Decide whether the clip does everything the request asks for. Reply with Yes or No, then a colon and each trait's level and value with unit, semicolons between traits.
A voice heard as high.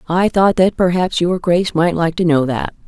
No: medium, 175 Hz